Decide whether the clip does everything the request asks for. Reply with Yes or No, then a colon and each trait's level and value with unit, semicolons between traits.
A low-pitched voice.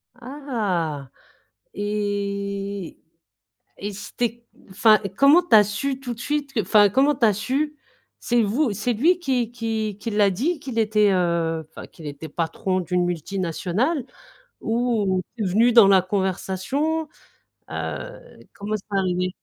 No: high, 210 Hz